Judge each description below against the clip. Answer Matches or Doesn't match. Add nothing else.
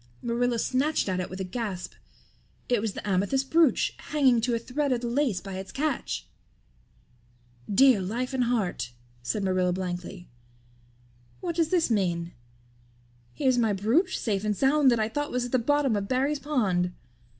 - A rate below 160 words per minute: Doesn't match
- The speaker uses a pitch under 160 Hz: Doesn't match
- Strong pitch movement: Matches